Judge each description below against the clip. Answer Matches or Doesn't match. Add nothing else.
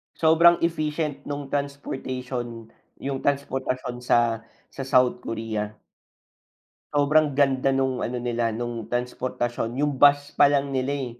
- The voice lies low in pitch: Matches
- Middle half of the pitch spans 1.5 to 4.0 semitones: Matches